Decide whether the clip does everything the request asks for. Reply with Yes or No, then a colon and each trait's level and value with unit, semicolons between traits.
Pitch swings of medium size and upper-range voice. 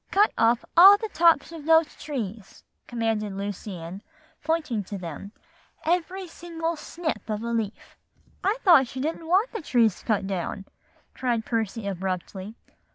No: wide, 8.4 semitones; high, 235 Hz